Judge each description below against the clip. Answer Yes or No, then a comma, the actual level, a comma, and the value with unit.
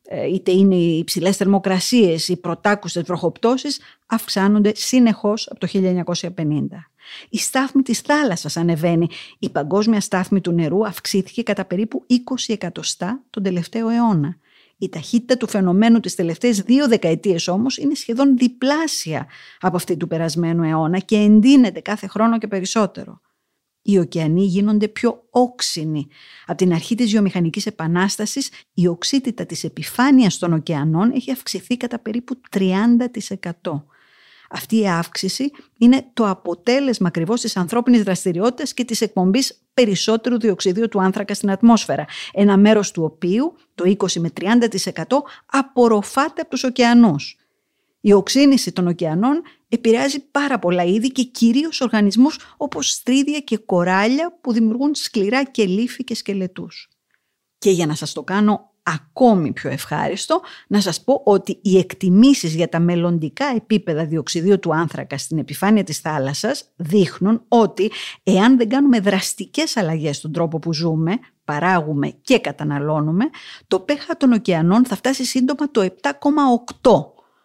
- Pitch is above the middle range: Yes, high, 205 Hz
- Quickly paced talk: No, average, 135 wpm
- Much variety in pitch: Yes, wide, 5.7 semitones